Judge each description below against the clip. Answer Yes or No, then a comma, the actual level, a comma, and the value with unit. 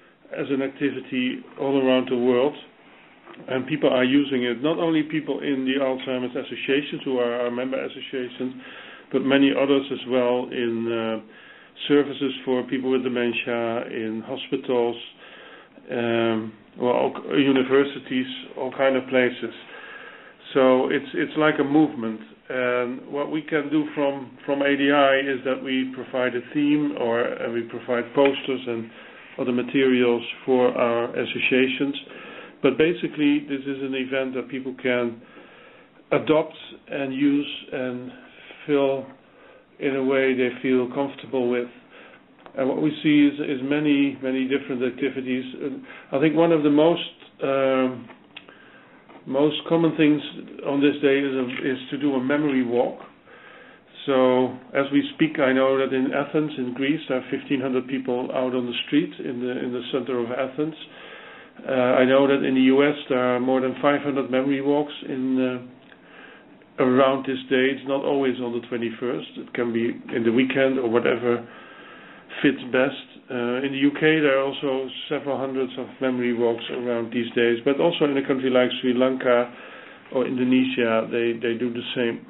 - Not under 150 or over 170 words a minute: Yes, average, 165 wpm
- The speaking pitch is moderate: No, low, 130 Hz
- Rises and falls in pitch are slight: Yes, narrow, 2.2 semitones